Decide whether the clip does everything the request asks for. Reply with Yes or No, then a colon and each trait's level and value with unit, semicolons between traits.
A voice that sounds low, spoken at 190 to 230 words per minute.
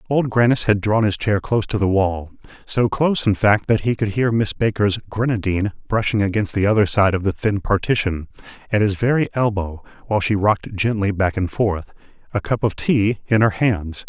Yes: low, 105 Hz; average, 200 wpm